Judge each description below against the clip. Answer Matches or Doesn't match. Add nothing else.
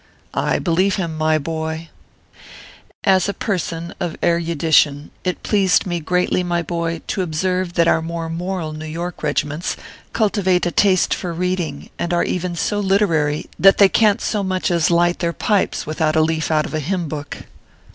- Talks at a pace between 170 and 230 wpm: Matches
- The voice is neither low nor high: Matches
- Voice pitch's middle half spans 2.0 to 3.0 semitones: Matches